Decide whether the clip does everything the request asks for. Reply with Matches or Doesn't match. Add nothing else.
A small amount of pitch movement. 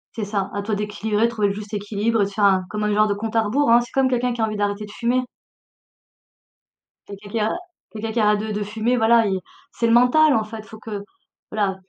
Matches